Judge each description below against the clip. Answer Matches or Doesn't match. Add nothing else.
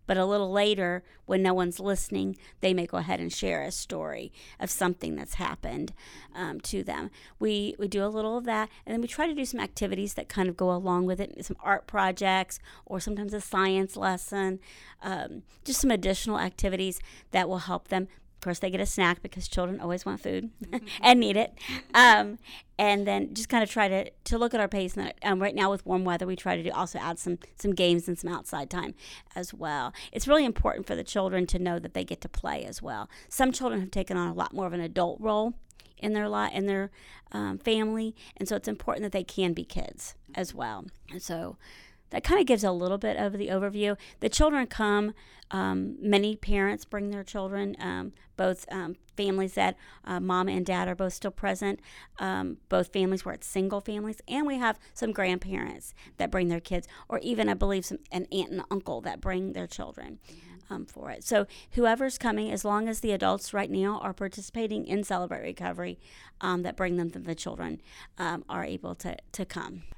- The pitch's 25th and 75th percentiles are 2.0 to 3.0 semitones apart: Matches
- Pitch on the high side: Matches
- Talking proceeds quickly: Matches